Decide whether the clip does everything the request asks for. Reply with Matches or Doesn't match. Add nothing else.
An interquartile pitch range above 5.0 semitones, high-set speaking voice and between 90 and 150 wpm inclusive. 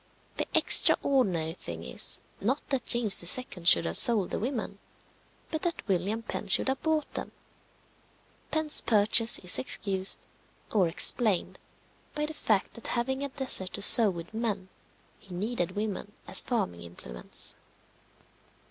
Matches